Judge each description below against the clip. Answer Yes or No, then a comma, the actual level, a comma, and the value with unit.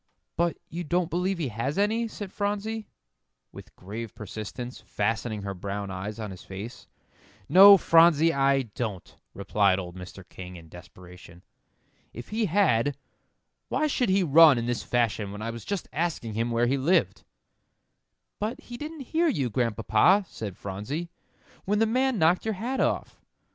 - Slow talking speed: No, average, 160 wpm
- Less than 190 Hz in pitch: Yes, low, 135 Hz